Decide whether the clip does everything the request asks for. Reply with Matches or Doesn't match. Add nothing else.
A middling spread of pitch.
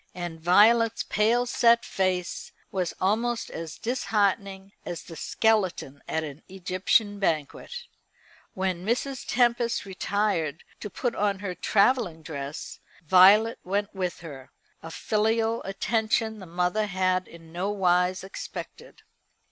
Matches